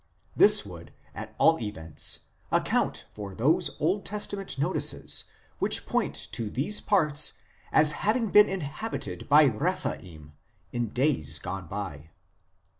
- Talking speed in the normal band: No, slow, 120 wpm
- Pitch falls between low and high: Yes, medium, 145 Hz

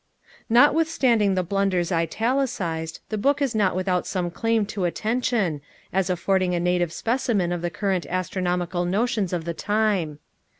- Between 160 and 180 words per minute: No, average, 145 wpm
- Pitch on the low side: No, high, 190 Hz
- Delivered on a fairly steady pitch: No, average, 4.0 semitones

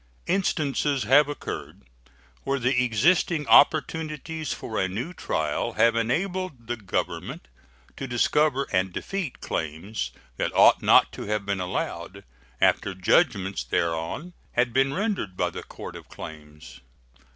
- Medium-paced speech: No, slow, 130 wpm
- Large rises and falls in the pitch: Yes, wide, 8.1 semitones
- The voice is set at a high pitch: No, low, 120 Hz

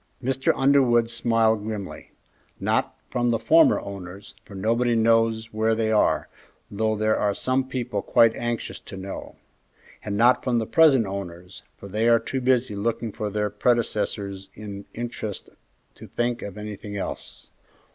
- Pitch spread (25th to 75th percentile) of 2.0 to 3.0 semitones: Yes, narrow, 2.6 semitones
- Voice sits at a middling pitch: No, low, 110 Hz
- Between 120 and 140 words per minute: No, average, 155 wpm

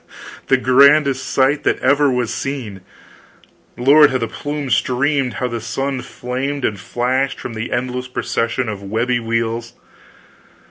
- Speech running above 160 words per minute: No, average, 140 wpm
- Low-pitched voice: Yes, low, 125 Hz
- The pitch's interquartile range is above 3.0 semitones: No, average, 2.7 semitones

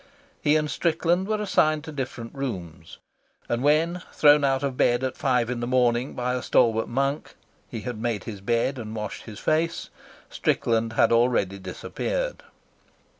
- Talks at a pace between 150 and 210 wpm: Yes, average, 165 wpm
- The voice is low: Yes, low, 125 Hz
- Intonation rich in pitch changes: No, average, 4.5 semitones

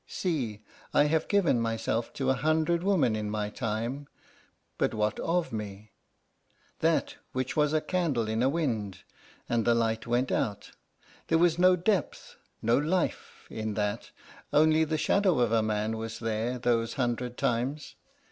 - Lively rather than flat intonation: Yes, wide, 5.9 semitones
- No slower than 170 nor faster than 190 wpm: No, average, 155 wpm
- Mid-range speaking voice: No, low, 120 Hz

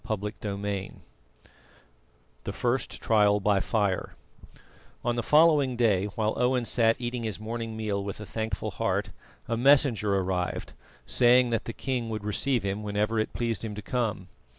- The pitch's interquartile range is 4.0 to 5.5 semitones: No, average, 2.7 semitones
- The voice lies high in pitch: No, low, 110 Hz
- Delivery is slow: No, average, 155 wpm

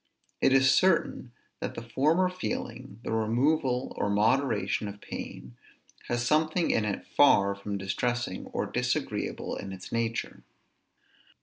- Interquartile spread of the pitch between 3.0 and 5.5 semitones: Yes, average, 4.8 semitones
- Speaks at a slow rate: Yes, slow, 130 wpm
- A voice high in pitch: No, low, 120 Hz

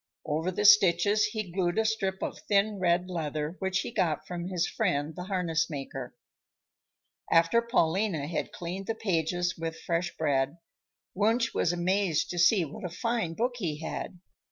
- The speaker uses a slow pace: No, average, 165 wpm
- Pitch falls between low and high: Yes, medium, 180 Hz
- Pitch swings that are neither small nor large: Yes, average, 3.8 semitones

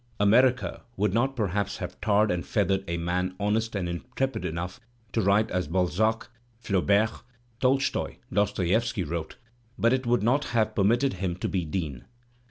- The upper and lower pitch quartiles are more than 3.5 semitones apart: Yes, average, 4.0 semitones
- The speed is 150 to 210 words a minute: Yes, average, 160 wpm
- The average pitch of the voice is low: Yes, low, 100 Hz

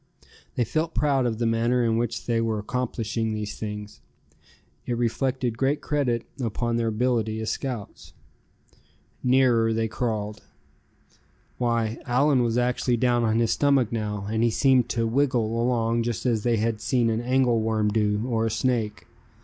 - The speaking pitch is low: Yes, low, 115 Hz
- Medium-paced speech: Yes, average, 160 wpm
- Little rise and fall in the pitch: Yes, narrow, 2.0 semitones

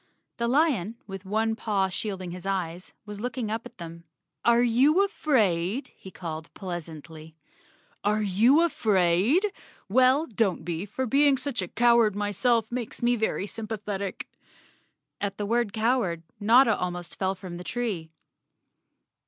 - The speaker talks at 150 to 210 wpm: No, average, 140 wpm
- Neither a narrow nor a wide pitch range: Yes, average, 4.7 semitones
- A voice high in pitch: Yes, high, 210 Hz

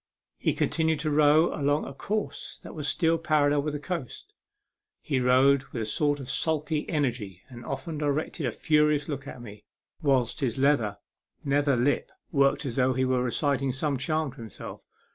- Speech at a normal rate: Yes, average, 180 wpm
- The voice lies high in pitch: No, medium, 140 Hz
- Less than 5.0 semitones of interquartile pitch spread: Yes, average, 2.9 semitones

